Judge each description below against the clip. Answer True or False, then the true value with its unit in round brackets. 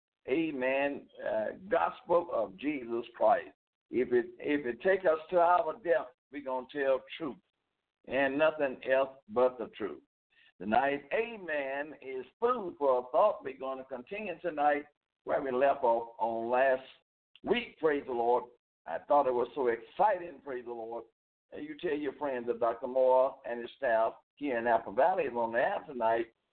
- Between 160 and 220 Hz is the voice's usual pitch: False (135 Hz)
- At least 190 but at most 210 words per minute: False (175 wpm)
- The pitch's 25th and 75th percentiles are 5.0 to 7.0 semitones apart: True (5.5 semitones)